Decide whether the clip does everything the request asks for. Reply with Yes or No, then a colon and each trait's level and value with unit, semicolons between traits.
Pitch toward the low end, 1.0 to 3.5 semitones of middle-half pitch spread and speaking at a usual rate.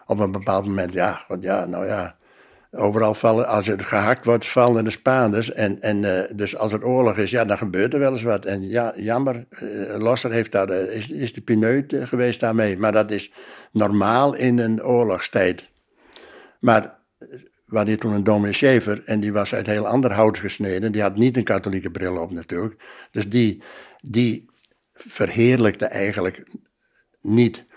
Yes: low, 110 Hz; average, 2.7 semitones; average, 175 wpm